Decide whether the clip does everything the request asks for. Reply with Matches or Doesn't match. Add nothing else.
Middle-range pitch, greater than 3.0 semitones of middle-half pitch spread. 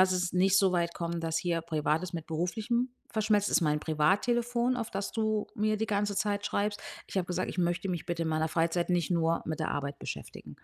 Matches